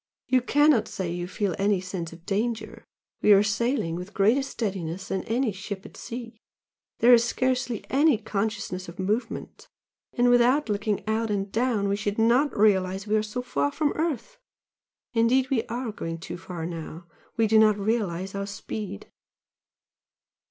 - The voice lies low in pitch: No, high, 215 Hz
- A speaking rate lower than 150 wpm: No, average, 165 wpm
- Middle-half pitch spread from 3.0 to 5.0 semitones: Yes, average, 3.9 semitones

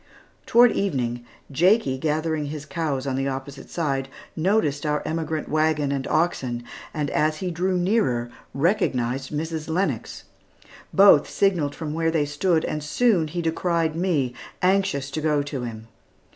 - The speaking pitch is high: No, medium, 155 Hz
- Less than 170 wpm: Yes, average, 145 wpm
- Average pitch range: Yes, average, 3.7 semitones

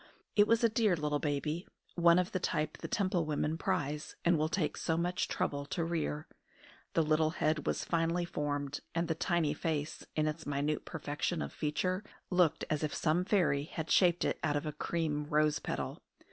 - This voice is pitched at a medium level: Yes, medium, 155 Hz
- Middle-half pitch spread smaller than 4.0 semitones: Yes, narrow, 2.5 semitones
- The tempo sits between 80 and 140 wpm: No, average, 190 wpm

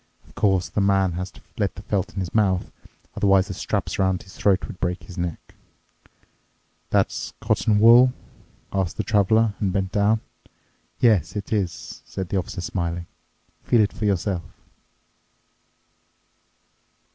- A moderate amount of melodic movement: No, narrow, 2.2 semitones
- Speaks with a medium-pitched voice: No, very low, 95 Hz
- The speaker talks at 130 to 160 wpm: Yes, average, 145 wpm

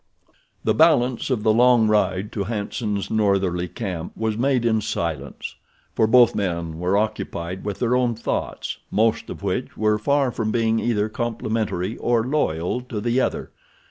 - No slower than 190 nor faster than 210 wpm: No, average, 160 wpm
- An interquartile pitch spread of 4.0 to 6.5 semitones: No, average, 3.3 semitones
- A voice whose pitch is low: Yes, low, 110 Hz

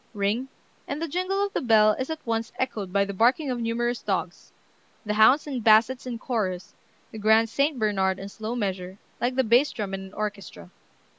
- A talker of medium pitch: No, high, 225 Hz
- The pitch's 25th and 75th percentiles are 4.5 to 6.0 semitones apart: No, average, 4.1 semitones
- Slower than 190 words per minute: No, average, 200 wpm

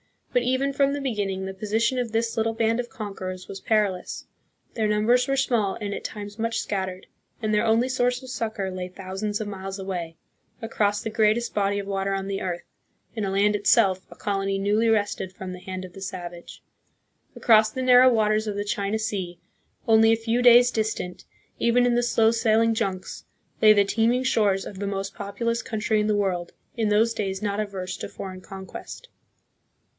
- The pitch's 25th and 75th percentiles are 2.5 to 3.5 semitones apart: Yes, average, 2.8 semitones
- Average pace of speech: Yes, average, 195 wpm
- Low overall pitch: No, high, 210 Hz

